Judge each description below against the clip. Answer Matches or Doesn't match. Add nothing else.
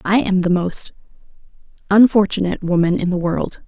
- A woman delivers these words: Matches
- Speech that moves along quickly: Doesn't match